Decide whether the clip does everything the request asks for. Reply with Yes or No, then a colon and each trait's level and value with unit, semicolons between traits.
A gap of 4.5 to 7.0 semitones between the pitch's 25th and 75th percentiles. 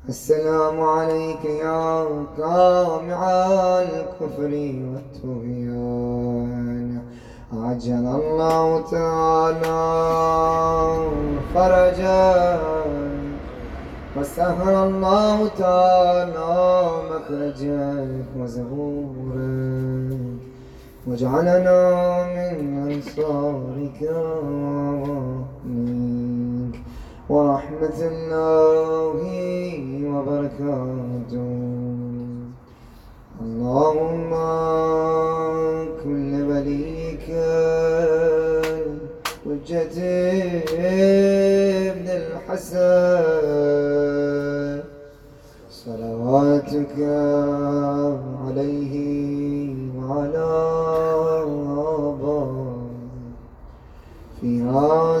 No: average, 3.7 semitones